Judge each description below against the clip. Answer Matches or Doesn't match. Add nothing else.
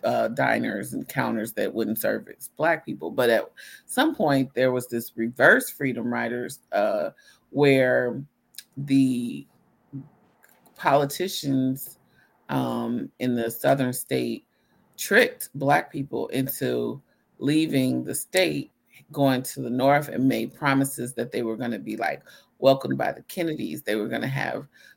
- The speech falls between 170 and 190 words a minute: Doesn't match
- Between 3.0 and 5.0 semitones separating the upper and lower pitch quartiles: Doesn't match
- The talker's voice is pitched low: Matches